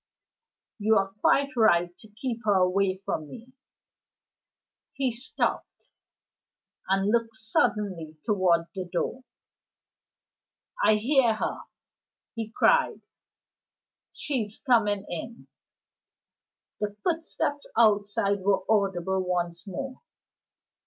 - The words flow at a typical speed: No, slow, 95 wpm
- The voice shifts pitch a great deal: No, average, 3.5 semitones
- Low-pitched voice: No, high, 210 Hz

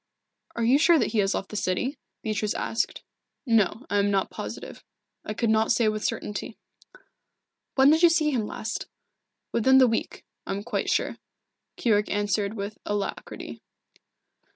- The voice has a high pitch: Yes, high, 220 Hz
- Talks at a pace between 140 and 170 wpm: Yes, average, 160 wpm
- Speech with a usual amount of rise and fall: Yes, average, 3.3 semitones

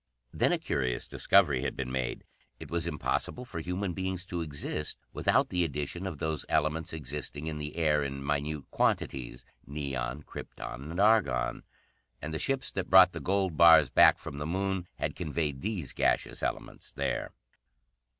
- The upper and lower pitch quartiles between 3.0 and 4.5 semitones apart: Yes, average, 4.0 semitones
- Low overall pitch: Yes, very low, 80 Hz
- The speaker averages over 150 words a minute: Yes, average, 165 wpm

